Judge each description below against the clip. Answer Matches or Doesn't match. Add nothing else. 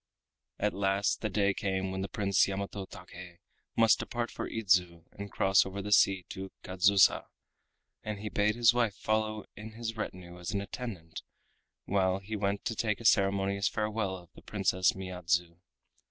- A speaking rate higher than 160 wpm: Matches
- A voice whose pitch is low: Matches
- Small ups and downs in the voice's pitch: Matches